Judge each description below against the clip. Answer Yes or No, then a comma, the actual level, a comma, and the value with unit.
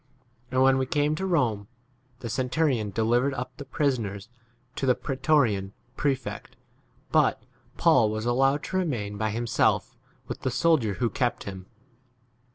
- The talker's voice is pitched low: Yes, low, 125 Hz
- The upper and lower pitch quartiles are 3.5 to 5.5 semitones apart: Yes, average, 4.2 semitones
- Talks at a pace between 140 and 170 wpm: Yes, average, 160 wpm